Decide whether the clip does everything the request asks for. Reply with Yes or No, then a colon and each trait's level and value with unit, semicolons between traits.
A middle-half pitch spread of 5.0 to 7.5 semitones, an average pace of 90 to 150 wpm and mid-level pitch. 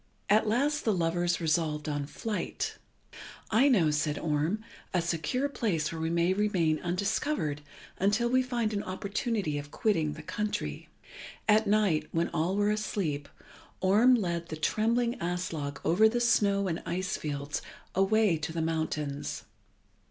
Yes: average, 5.3 semitones; average, 145 wpm; medium, 180 Hz